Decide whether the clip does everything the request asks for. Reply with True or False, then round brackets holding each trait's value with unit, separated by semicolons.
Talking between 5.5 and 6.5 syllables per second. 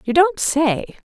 False (3.3 syllables/s)